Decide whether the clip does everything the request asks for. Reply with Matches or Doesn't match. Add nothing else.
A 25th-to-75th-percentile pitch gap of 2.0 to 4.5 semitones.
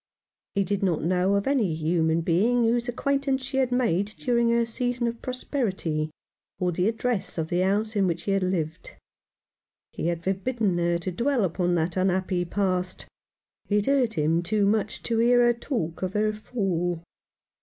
Doesn't match